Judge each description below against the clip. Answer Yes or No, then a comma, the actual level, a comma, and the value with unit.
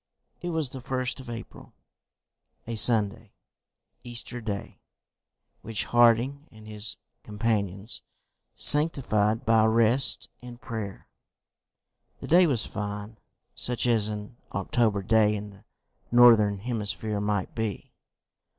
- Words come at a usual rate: No, slow, 115 wpm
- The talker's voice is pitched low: Yes, low, 110 Hz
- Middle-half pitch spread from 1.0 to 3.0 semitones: Yes, narrow, 2.6 semitones